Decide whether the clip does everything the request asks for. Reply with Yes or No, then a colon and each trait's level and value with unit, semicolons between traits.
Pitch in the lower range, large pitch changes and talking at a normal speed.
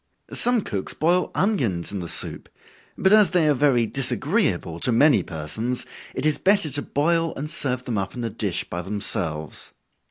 Yes: low, 130 Hz; wide, 8.8 semitones; average, 180 wpm